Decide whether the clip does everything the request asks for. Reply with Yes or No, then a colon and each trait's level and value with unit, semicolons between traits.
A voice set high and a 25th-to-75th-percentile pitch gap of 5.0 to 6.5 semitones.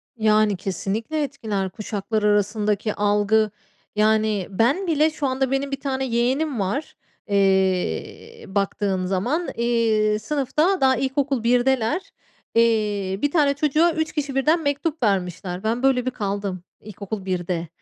Yes: high, 225 Hz; average, 5.3 semitones